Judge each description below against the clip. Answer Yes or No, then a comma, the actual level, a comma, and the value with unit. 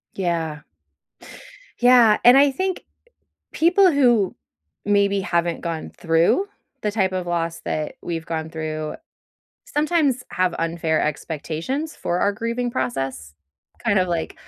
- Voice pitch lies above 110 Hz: Yes, medium, 185 Hz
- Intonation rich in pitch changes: Yes, wide, 7.0 semitones